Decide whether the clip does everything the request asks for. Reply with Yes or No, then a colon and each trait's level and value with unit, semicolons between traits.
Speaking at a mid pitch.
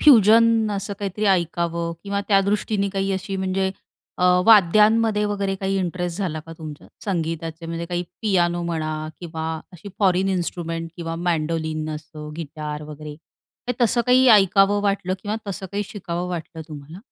Yes: medium, 180 Hz